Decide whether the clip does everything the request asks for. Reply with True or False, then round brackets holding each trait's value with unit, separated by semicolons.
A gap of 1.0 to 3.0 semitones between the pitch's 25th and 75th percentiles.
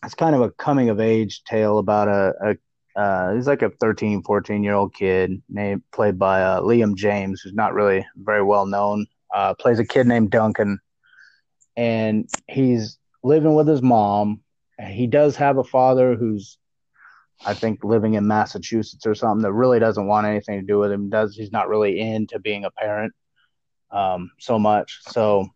True (2.4 semitones)